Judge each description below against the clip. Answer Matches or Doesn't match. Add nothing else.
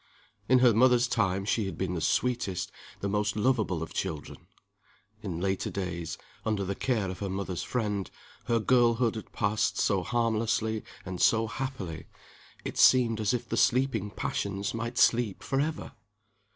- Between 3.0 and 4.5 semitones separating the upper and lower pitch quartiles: Matches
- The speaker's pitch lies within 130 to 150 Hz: Doesn't match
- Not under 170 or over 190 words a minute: Doesn't match